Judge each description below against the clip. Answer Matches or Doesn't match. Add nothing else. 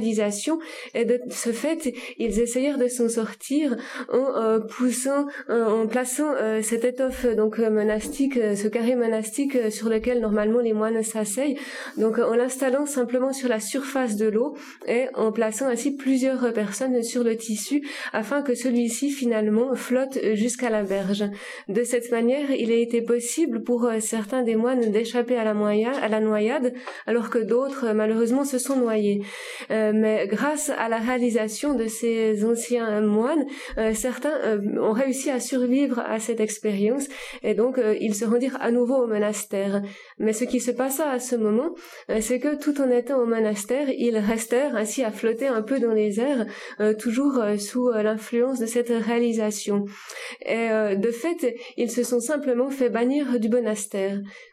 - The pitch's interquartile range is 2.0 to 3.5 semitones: Matches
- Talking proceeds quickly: Matches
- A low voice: Doesn't match